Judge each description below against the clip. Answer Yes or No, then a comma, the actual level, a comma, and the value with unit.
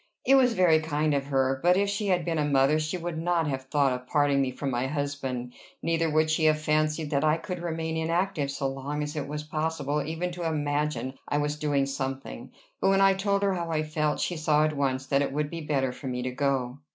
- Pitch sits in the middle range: Yes, medium, 150 Hz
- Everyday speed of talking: No, fast, 240 wpm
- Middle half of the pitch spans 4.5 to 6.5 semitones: No, average, 2.8 semitones